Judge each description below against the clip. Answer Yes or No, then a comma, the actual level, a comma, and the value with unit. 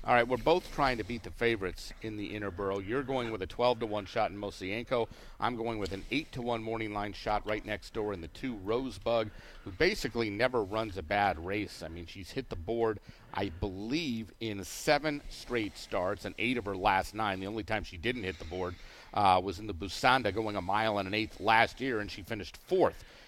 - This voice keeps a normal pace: No, fast, 230 wpm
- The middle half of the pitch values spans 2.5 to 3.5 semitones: Yes, average, 3.0 semitones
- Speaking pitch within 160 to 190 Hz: No, low, 105 Hz